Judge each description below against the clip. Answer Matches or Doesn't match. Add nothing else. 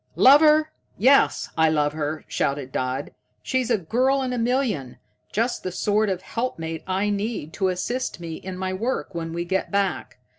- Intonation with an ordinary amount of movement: Doesn't match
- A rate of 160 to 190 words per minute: Matches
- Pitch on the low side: Doesn't match